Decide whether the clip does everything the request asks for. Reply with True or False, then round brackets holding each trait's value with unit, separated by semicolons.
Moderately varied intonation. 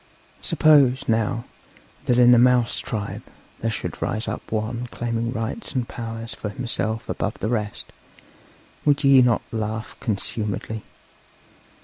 False (2.1 semitones)